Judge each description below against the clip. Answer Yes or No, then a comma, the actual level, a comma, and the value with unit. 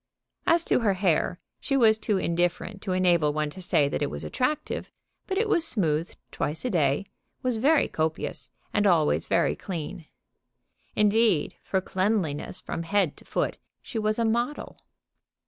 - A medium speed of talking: Yes, average, 165 wpm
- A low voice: No, high, 190 Hz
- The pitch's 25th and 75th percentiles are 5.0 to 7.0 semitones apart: Yes, wide, 5.4 semitones